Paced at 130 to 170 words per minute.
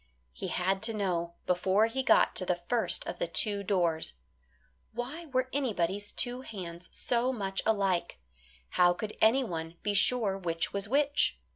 Yes: average, 155 wpm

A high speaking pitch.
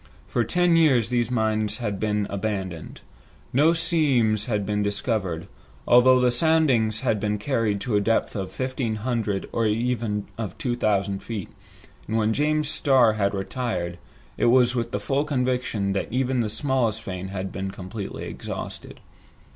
No: low, 110 Hz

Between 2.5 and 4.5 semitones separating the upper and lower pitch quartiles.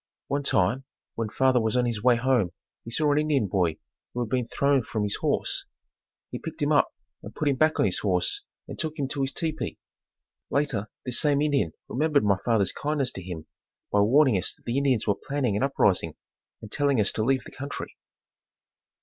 No: wide, 5.4 semitones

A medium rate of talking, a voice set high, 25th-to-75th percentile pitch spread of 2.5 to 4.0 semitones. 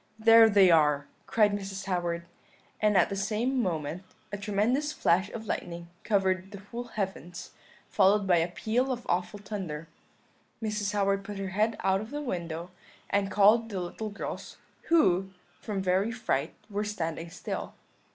Yes: average, 160 wpm; high, 200 Hz; average, 3.0 semitones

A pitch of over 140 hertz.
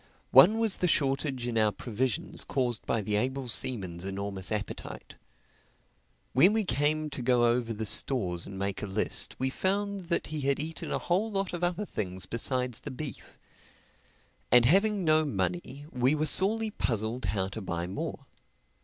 No: low, 130 Hz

